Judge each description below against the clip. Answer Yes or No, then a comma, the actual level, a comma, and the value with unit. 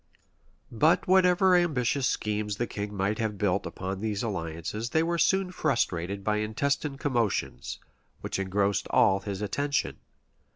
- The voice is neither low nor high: No, low, 110 Hz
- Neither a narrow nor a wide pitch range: No, wide, 6.4 semitones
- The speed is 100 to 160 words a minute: Yes, average, 140 wpm